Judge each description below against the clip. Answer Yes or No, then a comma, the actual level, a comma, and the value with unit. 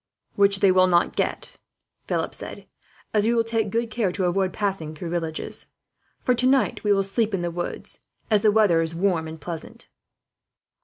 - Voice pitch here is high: Yes, high, 195 Hz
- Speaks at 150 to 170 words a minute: No, average, 185 wpm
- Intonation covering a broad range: No, average, 3.8 semitones